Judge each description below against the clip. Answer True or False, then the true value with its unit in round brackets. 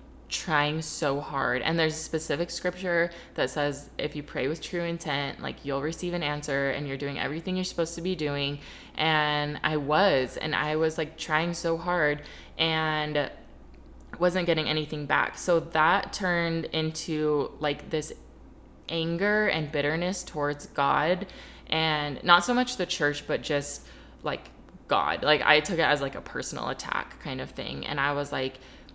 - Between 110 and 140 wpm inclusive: False (170 wpm)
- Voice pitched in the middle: True (155 Hz)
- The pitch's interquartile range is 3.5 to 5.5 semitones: False (2.5 semitones)